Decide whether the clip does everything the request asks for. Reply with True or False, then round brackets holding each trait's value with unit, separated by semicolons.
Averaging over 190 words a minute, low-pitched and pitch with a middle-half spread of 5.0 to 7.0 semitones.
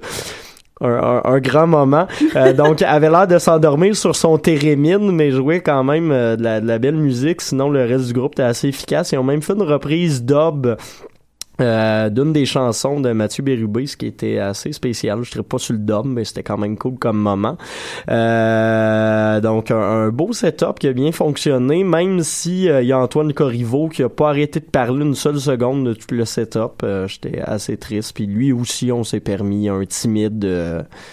True (210 wpm; 130 Hz; 5.3 semitones)